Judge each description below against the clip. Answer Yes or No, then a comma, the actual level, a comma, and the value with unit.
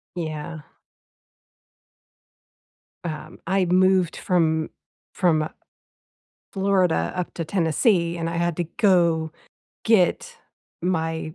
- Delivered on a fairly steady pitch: Yes, narrow, 2.3 semitones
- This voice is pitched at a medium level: Yes, medium, 170 Hz